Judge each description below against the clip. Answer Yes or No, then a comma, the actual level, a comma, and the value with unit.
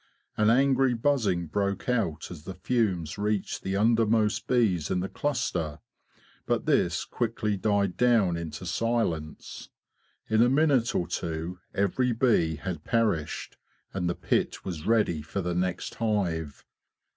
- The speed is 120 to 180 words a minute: Yes, average, 145 wpm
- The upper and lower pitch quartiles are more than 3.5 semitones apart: Yes, average, 5.0 semitones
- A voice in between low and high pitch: No, low, 100 Hz